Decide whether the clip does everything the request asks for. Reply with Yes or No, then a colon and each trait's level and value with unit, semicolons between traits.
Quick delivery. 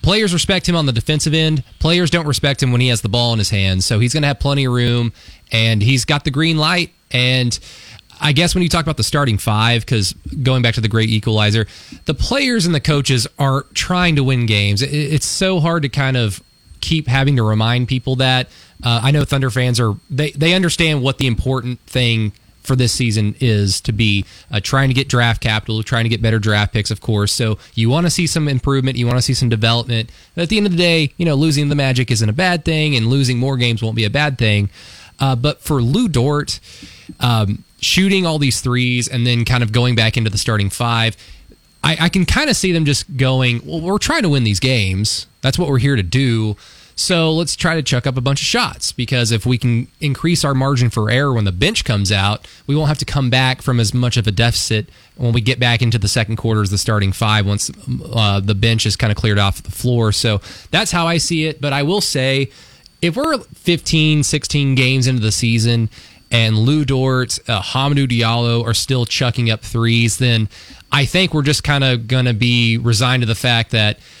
Yes: fast, 235 wpm